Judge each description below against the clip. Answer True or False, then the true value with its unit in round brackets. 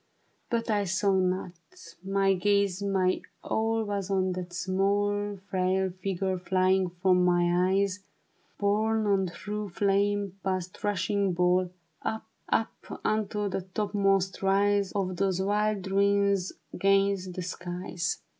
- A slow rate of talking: True (125 wpm)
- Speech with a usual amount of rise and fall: False (1.7 semitones)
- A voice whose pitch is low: False (195 Hz)